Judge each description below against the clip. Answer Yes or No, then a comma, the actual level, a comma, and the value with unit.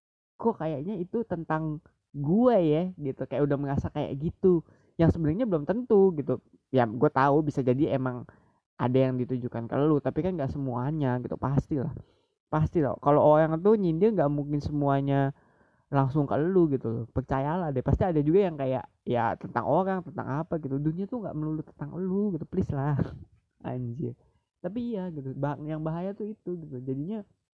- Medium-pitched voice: Yes, medium, 150 Hz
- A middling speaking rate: No, fast, 175 wpm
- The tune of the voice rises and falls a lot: No, average, 4.3 semitones